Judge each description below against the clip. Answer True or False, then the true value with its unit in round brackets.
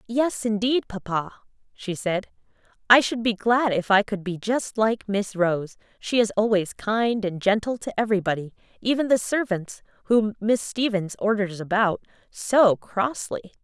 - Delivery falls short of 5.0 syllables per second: True (4.4 syllables/s)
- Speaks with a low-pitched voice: False (210 Hz)